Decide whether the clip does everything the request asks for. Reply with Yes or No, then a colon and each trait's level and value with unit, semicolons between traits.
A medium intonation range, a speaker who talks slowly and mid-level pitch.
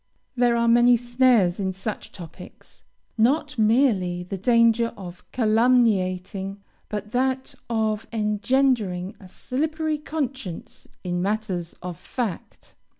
No: average, 4.7 semitones; slow, 110 wpm; high, 220 Hz